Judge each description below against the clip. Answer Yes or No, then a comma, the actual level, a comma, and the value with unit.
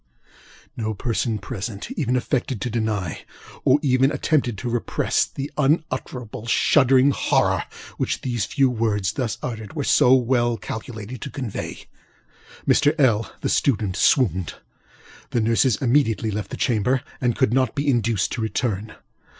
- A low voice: Yes, low, 120 Hz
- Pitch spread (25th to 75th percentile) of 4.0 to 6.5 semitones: No, average, 3.4 semitones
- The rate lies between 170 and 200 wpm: No, average, 140 wpm